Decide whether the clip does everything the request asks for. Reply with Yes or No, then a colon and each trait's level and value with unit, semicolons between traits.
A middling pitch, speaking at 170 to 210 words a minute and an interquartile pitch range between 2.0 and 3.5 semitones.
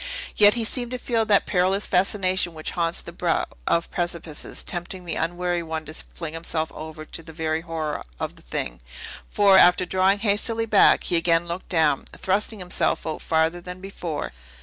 Yes: medium, 175 Hz; average, 180 wpm; average, 3.2 semitones